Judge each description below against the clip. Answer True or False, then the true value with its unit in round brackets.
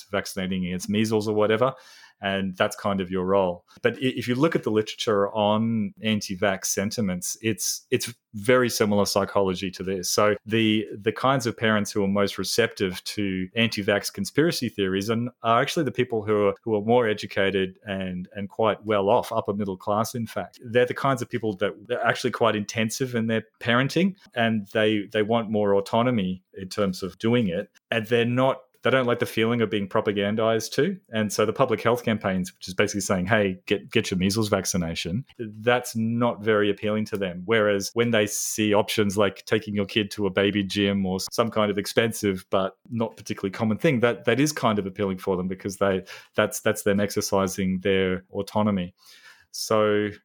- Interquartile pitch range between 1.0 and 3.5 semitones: True (2.6 semitones)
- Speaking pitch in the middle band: False (105 Hz)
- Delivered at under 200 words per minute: True (190 wpm)